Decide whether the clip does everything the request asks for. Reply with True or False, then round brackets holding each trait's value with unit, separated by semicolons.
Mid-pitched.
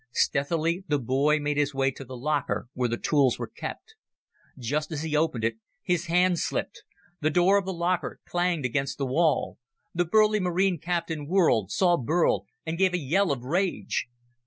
True (155 Hz)